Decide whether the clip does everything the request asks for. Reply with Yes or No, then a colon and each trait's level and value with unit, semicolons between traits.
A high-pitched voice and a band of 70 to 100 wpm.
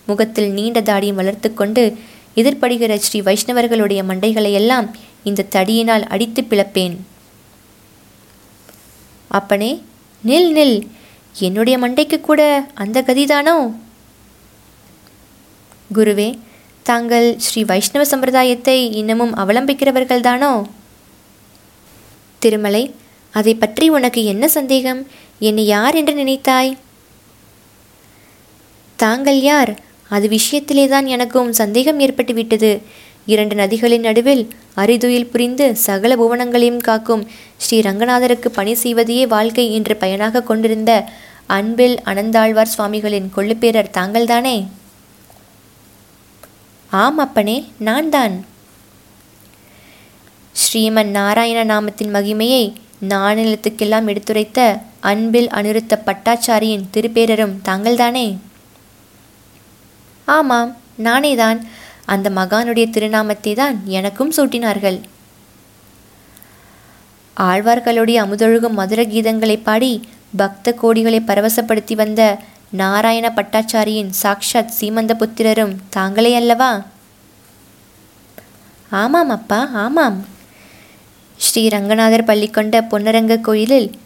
Yes: high, 220 Hz; average, 80 wpm